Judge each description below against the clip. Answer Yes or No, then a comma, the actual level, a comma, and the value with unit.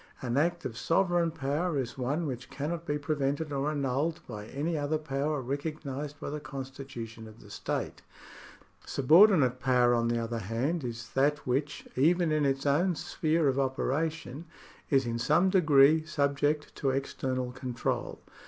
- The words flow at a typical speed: Yes, average, 155 wpm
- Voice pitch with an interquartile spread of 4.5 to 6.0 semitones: No, average, 3.3 semitones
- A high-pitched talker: No, medium, 140 Hz